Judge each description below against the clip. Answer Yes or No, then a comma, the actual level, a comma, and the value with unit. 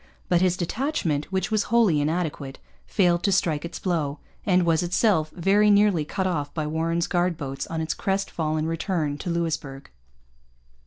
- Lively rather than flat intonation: No, average, 3.4 semitones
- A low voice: No, medium, 170 Hz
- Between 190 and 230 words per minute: No, average, 165 wpm